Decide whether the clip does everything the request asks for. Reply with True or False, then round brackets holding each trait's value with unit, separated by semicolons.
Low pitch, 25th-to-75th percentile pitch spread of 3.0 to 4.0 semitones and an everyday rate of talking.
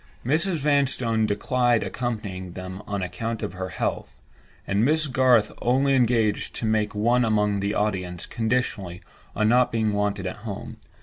True (110 Hz; 3.6 semitones; 150 wpm)